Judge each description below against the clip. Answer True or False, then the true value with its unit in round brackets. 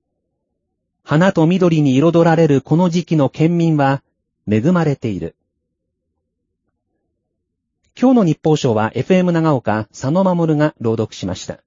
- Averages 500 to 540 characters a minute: False (220 characters per minute)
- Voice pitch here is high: False (140 Hz)